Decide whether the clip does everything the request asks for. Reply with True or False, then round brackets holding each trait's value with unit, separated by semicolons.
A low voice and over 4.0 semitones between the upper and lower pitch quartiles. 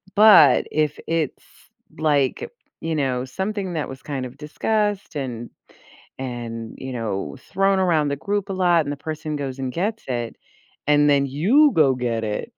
False (145 Hz; 5.6 semitones)